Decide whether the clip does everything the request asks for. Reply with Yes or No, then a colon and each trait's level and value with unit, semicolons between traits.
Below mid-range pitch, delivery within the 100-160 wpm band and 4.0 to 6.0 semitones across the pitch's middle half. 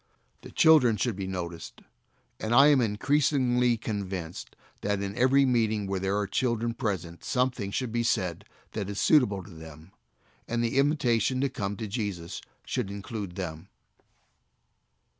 Yes: low, 105 Hz; average, 150 wpm; average, 4.4 semitones